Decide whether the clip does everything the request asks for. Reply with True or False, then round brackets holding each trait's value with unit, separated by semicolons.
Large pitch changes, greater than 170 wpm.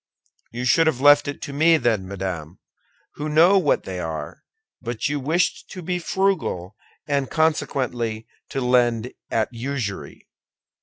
False (5.8 semitones; 145 wpm)